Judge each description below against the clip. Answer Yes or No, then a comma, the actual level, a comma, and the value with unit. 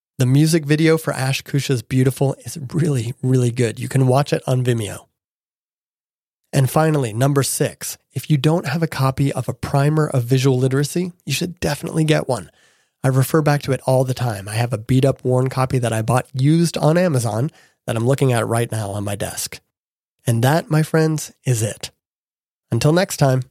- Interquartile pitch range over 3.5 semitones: No, average, 3.2 semitones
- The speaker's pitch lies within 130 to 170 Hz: Yes, low, 135 Hz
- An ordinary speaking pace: Yes, average, 195 wpm